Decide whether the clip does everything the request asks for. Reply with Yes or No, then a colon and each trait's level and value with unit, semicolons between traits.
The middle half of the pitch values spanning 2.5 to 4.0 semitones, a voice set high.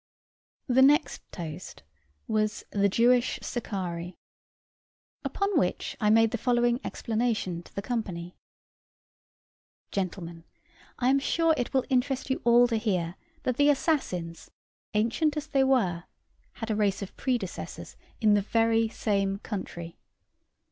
No: average, 4.8 semitones; high, 225 Hz